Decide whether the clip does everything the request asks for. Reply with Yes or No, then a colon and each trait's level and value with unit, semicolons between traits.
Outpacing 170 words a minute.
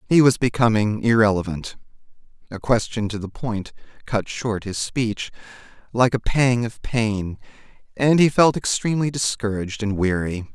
No: average, 140 wpm